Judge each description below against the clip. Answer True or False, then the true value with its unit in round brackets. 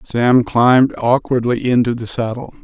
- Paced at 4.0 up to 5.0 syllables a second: True (4.5 syllables/s)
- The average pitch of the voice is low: True (120 Hz)